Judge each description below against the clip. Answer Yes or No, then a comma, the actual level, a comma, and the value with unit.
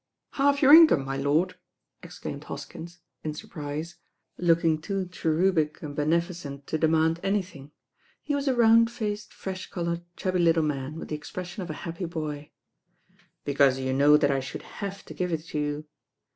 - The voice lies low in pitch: No, medium, 165 Hz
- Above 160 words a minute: Yes, average, 170 wpm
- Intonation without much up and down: No, average, 3.9 semitones